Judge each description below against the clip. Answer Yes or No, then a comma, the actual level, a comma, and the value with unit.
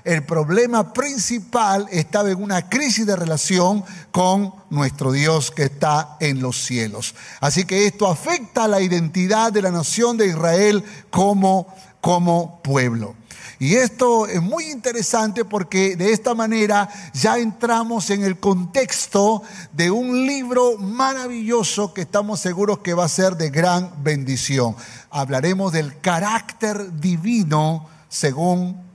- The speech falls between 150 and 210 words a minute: No, average, 135 wpm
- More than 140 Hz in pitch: Yes, high, 190 Hz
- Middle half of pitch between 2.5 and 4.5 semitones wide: No, average, 5.3 semitones